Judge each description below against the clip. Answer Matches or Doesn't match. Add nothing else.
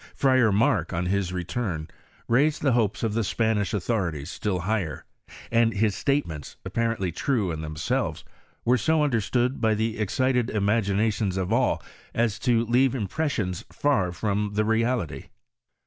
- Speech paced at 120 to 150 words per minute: Matches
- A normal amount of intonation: Matches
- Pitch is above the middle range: Doesn't match